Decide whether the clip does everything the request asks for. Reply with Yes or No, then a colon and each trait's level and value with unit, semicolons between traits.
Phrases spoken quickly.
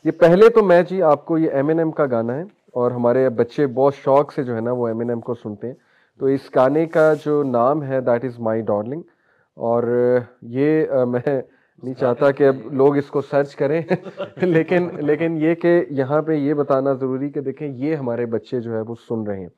Yes: fast, 225 wpm